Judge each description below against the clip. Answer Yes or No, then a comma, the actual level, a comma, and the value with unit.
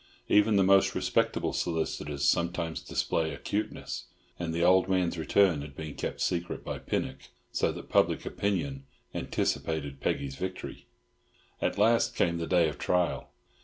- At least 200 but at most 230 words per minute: No, average, 145 wpm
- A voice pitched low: Yes, very low, 85 Hz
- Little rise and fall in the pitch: No, average, 3.3 semitones